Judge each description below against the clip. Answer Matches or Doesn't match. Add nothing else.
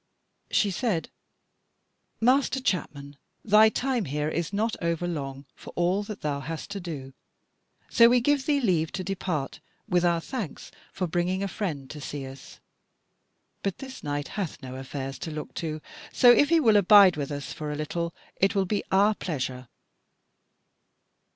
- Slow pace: Doesn't match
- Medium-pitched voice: Matches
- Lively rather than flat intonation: Matches